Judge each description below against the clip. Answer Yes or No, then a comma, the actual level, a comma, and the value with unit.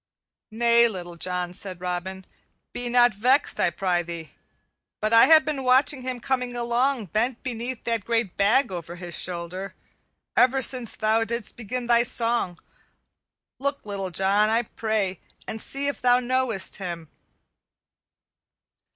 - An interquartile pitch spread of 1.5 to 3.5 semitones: No, average, 4.9 semitones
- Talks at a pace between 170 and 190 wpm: No, average, 140 wpm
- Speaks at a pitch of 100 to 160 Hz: No, high, 225 Hz